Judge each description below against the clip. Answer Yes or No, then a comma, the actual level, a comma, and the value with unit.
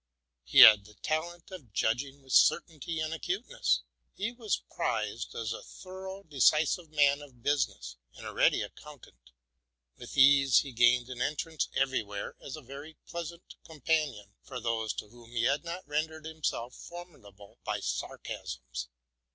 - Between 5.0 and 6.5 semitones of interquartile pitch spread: Yes, wide, 5.6 semitones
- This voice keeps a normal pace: Yes, average, 150 wpm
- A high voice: No, medium, 140 Hz